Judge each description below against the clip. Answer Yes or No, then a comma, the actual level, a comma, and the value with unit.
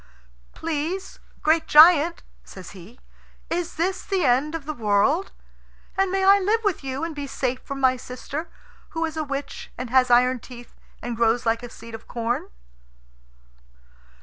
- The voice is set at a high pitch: Yes, very high, 280 Hz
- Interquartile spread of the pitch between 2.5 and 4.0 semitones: No, average, 5.3 semitones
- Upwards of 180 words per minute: No, average, 165 wpm